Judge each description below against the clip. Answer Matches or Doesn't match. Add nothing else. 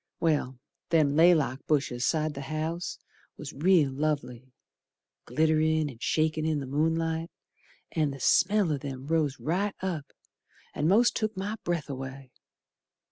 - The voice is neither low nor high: Matches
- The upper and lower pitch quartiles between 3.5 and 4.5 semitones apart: Doesn't match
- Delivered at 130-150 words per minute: Matches